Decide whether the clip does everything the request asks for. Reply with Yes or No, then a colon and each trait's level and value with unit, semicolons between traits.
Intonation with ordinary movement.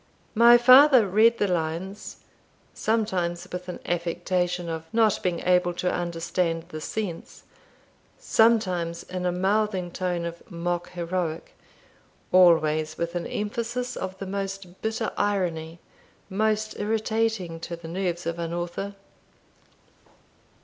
Yes: average, 3.7 semitones